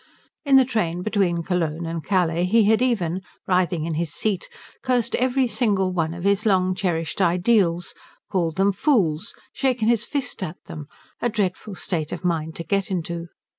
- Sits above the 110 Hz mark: Yes, medium, 185 Hz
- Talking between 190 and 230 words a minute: No, average, 170 wpm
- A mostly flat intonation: No, average, 4.4 semitones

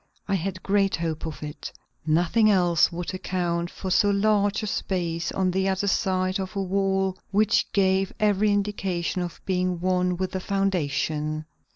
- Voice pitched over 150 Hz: Yes, medium, 185 Hz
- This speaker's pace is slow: No, average, 165 wpm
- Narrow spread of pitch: Yes, narrow, 2.1 semitones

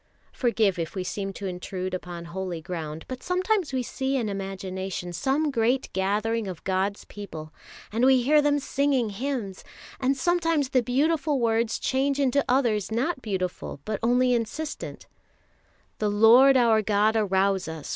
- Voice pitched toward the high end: Yes, high, 225 Hz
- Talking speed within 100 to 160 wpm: Yes, average, 155 wpm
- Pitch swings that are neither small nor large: No, wide, 5.8 semitones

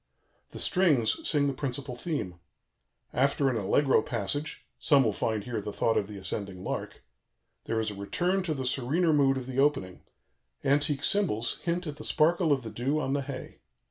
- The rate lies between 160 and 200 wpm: Yes, average, 185 wpm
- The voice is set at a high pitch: No, low, 135 Hz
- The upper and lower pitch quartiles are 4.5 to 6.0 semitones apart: Yes, average, 5.0 semitones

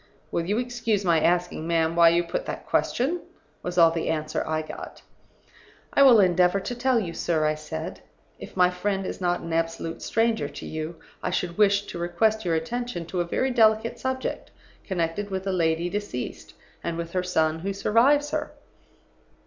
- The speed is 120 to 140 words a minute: No, average, 185 wpm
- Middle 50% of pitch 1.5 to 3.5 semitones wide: No, average, 4.7 semitones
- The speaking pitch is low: No, medium, 180 Hz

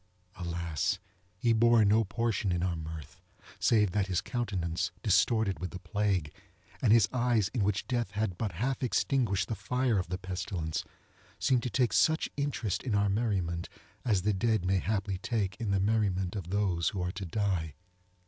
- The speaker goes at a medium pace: Yes, average, 175 wpm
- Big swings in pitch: No, average, 3.7 semitones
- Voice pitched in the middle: No, low, 100 Hz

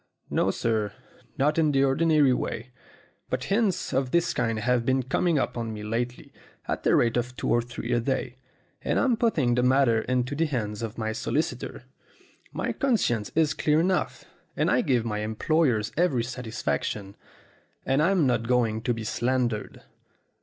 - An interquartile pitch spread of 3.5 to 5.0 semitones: Yes, average, 4.4 semitones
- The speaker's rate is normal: Yes, average, 170 wpm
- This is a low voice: Yes, low, 125 Hz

